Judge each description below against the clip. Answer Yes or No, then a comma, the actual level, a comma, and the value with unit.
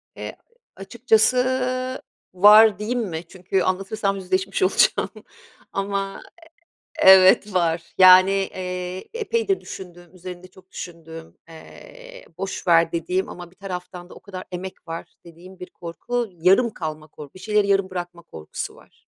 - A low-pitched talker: No, medium, 185 Hz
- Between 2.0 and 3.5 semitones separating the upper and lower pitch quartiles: Yes, narrow, 2.6 semitones